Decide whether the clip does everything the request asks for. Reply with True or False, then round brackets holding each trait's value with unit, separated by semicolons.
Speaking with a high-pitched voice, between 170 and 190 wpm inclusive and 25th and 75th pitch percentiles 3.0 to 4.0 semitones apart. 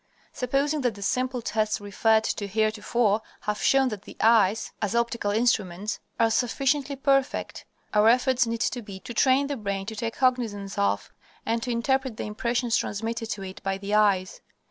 True (225 Hz; 175 wpm; 3.3 semitones)